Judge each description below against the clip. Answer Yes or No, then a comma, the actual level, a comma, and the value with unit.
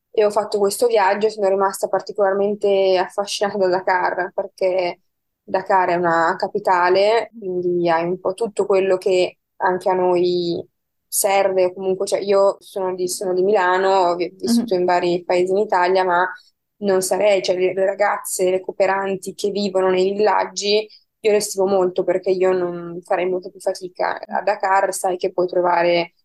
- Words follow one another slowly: No, average, 160 wpm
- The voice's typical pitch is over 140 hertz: Yes, high, 190 Hz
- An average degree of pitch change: No, narrow, 1.6 semitones